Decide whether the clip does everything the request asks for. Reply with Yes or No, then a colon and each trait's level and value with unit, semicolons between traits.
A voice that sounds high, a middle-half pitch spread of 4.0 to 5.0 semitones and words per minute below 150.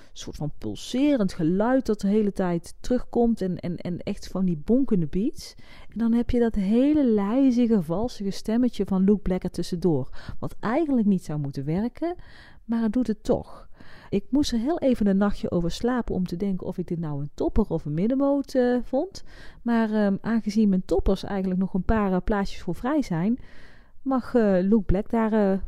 No: high, 210 Hz; average, 4.5 semitones; fast, 200 wpm